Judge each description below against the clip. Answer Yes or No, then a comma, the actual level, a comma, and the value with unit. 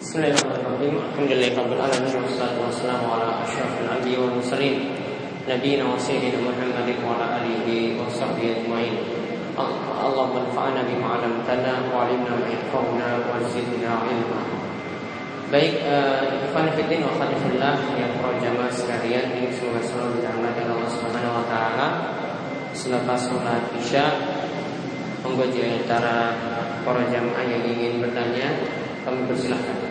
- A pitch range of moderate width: No, narrow, 1.5 semitones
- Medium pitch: No, low, 125 Hz